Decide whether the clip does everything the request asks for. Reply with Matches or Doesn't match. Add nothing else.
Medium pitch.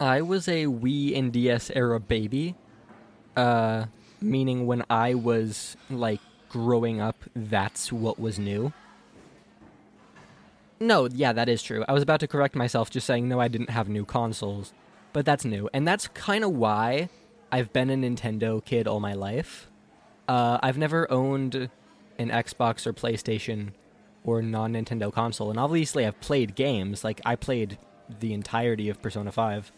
Doesn't match